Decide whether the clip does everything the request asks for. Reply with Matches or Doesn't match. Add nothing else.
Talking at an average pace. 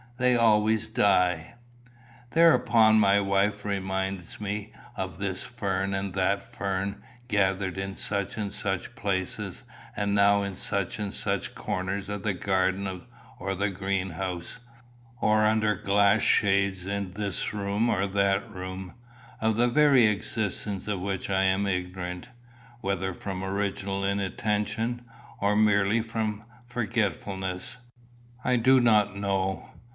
Doesn't match